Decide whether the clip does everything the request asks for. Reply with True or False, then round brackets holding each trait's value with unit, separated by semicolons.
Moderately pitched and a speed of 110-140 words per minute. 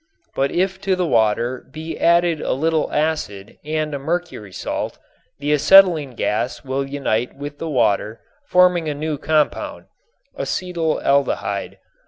True (150 Hz; 135 wpm)